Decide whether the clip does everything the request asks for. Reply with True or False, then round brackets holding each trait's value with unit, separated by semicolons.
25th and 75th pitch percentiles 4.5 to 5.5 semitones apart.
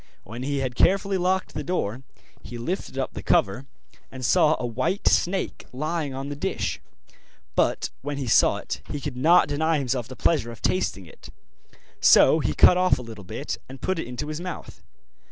True (5.1 semitones)